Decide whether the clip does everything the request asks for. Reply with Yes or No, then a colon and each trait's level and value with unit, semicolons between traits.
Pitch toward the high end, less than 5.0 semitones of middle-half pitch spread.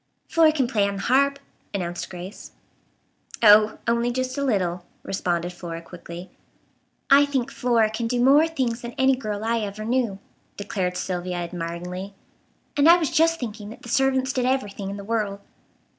No: high, 220 Hz; wide, 5.6 semitones